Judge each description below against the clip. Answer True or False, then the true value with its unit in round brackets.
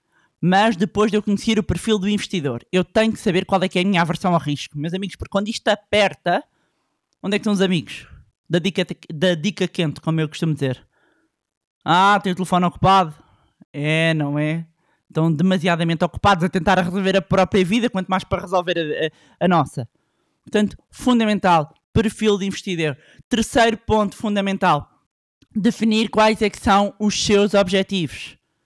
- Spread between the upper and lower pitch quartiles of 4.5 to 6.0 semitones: False (3.8 semitones)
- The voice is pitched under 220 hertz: True (190 Hz)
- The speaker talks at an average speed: True (175 wpm)